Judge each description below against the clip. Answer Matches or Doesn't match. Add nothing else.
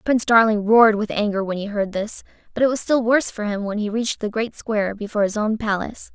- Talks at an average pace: Doesn't match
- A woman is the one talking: Matches